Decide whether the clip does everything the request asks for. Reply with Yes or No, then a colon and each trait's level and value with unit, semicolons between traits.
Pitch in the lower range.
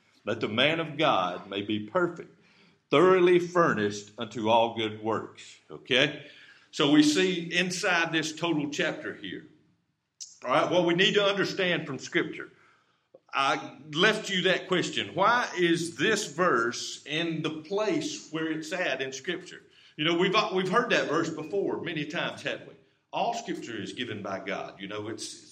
No: medium, 170 Hz